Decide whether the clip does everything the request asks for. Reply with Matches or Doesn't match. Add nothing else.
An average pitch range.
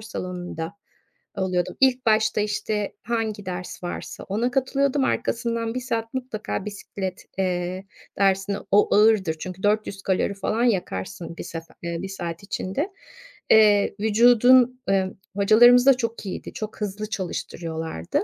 Matches